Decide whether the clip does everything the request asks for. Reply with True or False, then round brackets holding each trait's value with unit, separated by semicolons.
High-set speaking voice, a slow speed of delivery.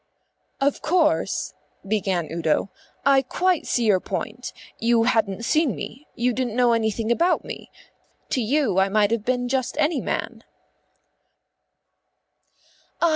True (240 Hz; 130 wpm)